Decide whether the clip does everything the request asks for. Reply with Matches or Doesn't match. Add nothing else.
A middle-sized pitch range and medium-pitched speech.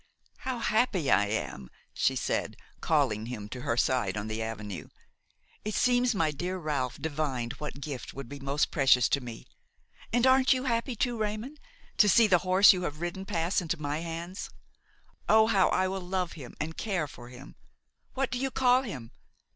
Doesn't match